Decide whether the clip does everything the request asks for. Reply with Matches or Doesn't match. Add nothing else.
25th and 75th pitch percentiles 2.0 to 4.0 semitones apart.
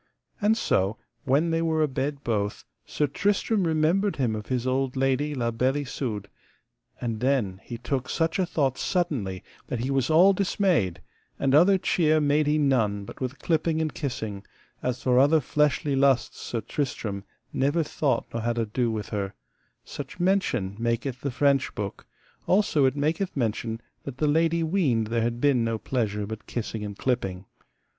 Doesn't match